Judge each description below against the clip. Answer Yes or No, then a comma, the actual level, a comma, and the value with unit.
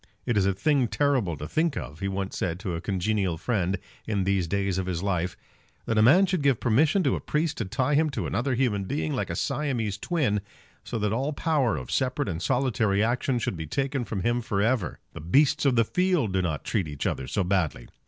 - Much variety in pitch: Yes, wide, 6.3 semitones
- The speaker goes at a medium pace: No, fast, 230 wpm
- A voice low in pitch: Yes, low, 110 Hz